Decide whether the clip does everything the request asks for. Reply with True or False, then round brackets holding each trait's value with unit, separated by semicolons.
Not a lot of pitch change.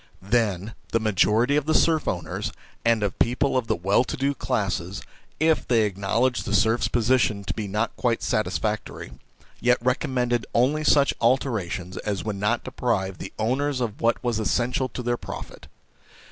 False (3.4 semitones)